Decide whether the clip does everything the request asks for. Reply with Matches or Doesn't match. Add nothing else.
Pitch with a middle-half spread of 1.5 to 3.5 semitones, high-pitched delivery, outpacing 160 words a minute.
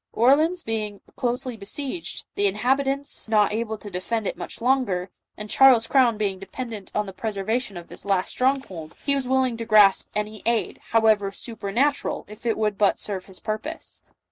Doesn't match